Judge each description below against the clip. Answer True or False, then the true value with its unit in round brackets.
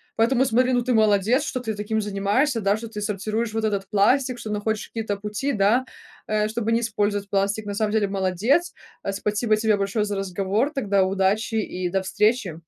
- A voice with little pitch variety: True (2.3 semitones)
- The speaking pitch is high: True (210 Hz)